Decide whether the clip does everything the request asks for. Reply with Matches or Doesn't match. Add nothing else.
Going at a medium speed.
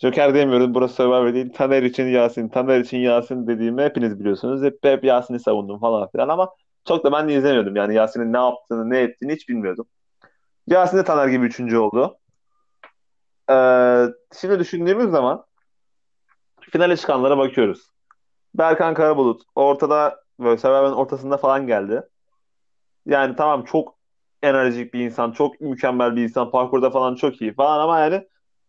Doesn't match